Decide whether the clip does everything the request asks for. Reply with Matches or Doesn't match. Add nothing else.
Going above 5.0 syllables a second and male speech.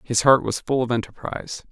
Matches